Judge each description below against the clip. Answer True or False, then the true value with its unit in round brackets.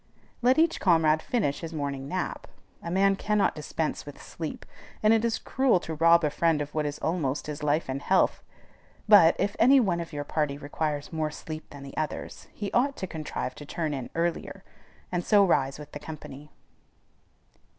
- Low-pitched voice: False (160 Hz)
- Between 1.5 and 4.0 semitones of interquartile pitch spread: False (4.4 semitones)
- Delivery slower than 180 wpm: False (190 wpm)